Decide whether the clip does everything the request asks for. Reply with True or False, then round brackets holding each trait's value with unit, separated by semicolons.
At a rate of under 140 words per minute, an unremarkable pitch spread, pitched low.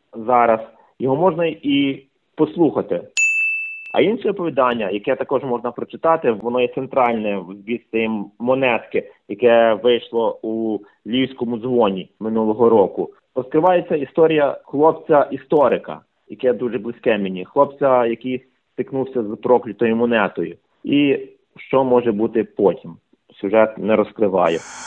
True (110 wpm; 3.8 semitones; 125 Hz)